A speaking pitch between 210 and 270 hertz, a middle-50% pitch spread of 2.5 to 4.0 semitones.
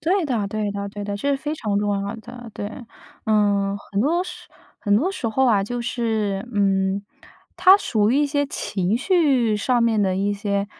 No: high, 215 Hz; average, 4.6 semitones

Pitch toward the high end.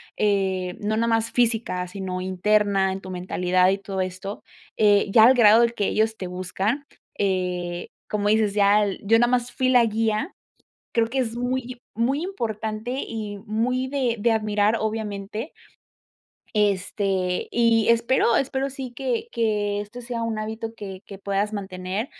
Yes: high, 215 Hz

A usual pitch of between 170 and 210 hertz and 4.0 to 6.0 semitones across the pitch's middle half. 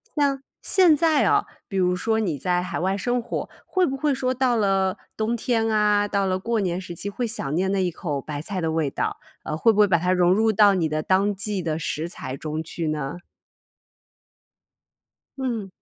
Yes: high, 195 Hz; average, 4.7 semitones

